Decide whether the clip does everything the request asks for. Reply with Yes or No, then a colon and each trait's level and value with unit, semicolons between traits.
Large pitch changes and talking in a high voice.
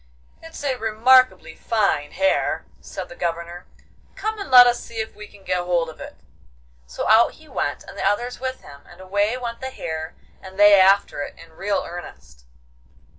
Yes: wide, 5.9 semitones; high, 205 Hz